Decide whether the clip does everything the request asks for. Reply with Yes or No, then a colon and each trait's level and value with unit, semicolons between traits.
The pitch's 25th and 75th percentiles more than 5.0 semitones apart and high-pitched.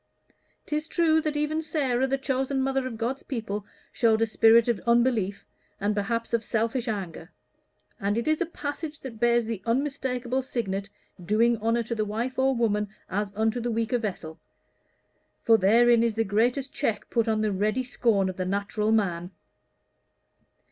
No: average, 3.6 semitones; high, 230 Hz